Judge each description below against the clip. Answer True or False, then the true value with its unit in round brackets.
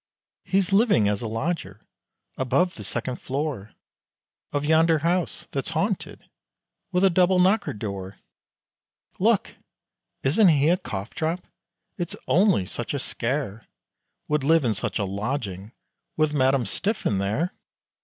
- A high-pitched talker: False (140 Hz)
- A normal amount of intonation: False (8.4 semitones)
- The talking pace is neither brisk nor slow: False (130 wpm)